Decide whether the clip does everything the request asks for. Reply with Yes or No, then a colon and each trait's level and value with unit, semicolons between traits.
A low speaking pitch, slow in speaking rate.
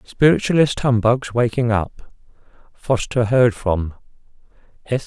Yes: low, 115 Hz; slow, 70 wpm